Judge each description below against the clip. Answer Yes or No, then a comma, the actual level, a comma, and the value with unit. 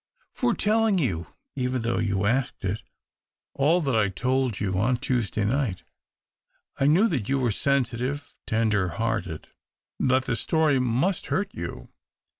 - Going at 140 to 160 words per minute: Yes, average, 150 wpm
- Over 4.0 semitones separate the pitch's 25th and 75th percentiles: Yes, average, 4.7 semitones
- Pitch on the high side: No, low, 125 Hz